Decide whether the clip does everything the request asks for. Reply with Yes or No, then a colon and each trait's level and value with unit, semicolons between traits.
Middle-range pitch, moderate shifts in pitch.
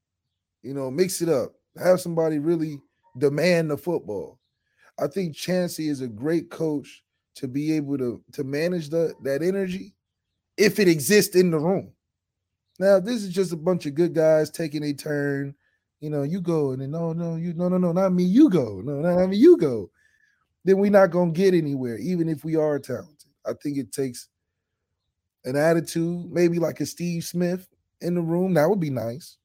Yes: medium, 160 Hz; average, 4.2 semitones